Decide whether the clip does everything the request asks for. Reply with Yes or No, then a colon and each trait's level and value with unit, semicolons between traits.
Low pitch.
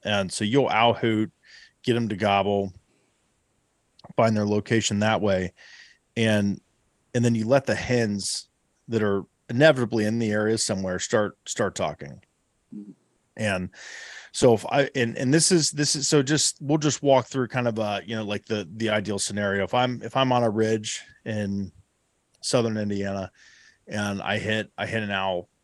Yes: low, 110 Hz